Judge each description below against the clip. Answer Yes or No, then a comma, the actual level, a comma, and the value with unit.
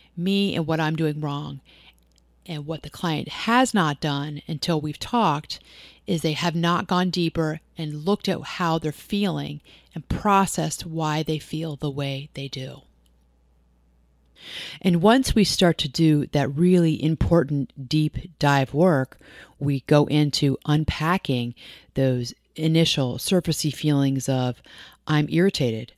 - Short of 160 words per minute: Yes, average, 140 wpm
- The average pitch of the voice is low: No, medium, 150 Hz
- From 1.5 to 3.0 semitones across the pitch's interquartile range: No, average, 3.6 semitones